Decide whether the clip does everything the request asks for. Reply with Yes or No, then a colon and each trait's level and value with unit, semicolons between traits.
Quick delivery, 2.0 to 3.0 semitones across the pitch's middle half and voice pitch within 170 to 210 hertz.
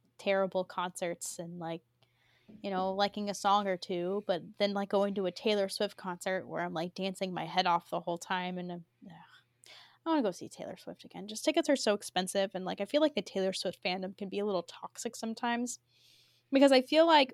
Yes: fast, 230 wpm; narrow, 2.6 semitones; high, 190 Hz